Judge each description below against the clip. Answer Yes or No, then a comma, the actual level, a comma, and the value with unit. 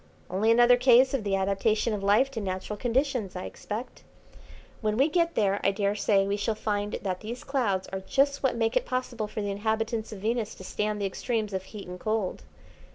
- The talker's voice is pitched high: Yes, high, 215 Hz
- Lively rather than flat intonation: No, average, 3.2 semitones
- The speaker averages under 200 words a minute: No, fast, 205 wpm